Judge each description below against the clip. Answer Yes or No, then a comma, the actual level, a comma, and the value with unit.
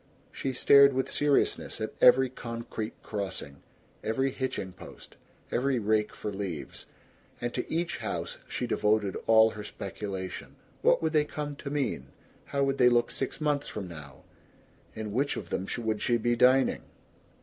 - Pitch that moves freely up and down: No, average, 4.6 semitones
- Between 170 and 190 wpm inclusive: No, average, 160 wpm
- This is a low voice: Yes, low, 120 Hz